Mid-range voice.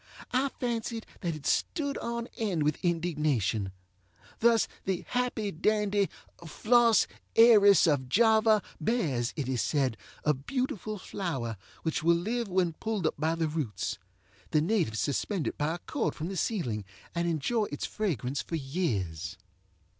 Yes: medium, 170 Hz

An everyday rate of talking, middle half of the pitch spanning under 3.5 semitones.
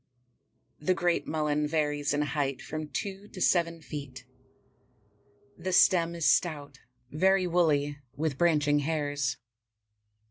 No: slow, 115 wpm; average, 2.8 semitones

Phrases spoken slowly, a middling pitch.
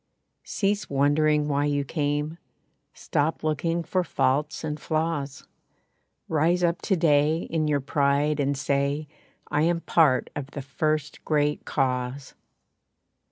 Yes: slow, 125 wpm; medium, 150 Hz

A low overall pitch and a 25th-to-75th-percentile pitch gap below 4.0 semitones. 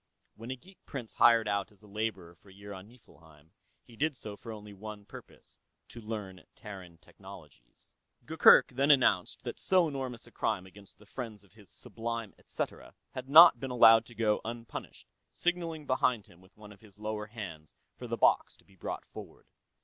Yes: low, 110 Hz; average, 3.4 semitones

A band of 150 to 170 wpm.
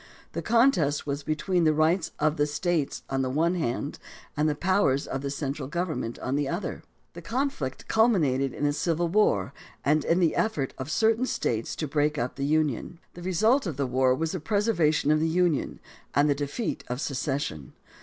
No: average, 195 wpm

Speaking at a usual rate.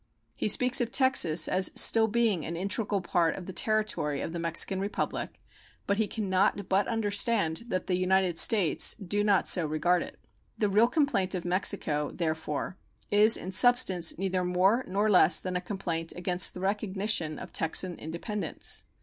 Yes: average, 170 wpm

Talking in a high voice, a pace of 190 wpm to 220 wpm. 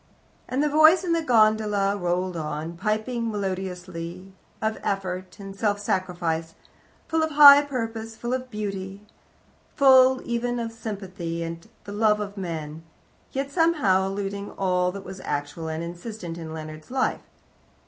No: high, 200 Hz; average, 145 wpm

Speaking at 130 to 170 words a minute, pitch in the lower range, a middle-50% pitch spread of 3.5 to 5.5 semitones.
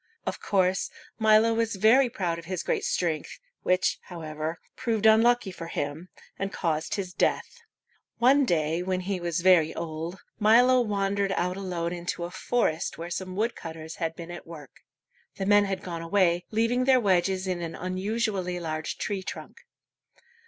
No: average, 160 wpm; medium, 185 Hz; average, 4.0 semitones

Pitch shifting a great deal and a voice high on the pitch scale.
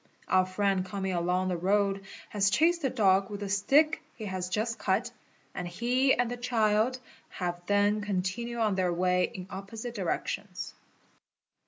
No: average, 3.6 semitones; high, 200 Hz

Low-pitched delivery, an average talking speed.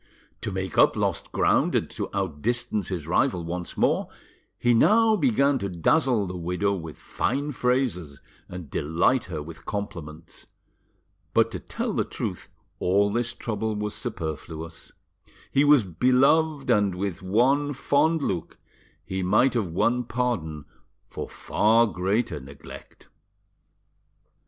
No: low, 100 Hz; slow, 130 wpm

